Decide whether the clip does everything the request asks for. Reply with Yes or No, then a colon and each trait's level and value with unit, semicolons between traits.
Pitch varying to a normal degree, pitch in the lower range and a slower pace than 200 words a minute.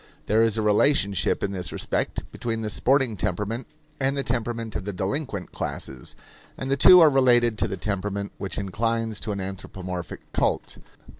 Yes: average, 3.5 semitones; low, 110 Hz; average, 170 wpm